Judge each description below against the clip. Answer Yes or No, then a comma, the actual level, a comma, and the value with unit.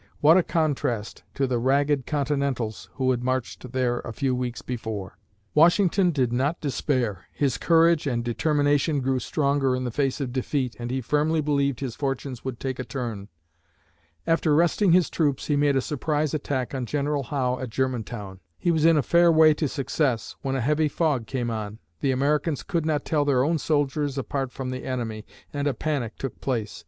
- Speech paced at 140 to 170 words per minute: No, average, 190 wpm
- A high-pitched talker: No, low, 135 Hz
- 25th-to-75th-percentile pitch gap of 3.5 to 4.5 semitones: No, average, 3.0 semitones